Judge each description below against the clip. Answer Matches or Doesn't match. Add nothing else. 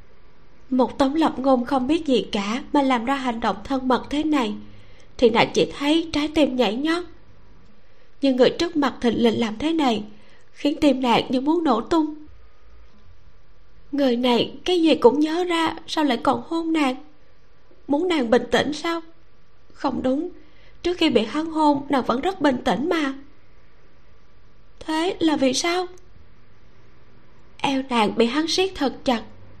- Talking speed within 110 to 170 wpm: Matches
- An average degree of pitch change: Matches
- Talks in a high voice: Matches